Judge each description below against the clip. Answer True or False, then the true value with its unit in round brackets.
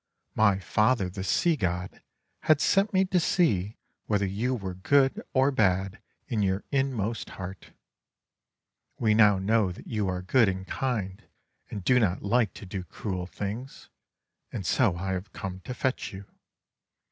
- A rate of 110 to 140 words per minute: False (160 wpm)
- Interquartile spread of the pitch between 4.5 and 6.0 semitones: True (4.9 semitones)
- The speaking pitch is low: True (105 Hz)